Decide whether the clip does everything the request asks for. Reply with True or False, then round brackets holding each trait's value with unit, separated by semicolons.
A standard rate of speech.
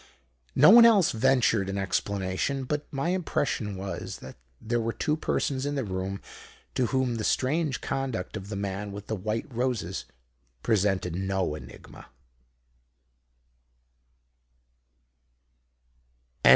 False (120 wpm)